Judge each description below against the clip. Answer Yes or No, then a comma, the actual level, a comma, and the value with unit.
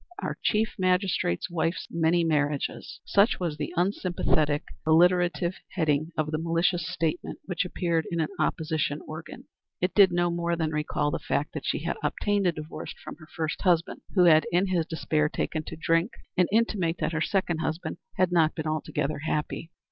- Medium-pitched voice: Yes, medium, 165 Hz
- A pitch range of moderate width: No, narrow, 2.3 semitones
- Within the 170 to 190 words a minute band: Yes, average, 180 wpm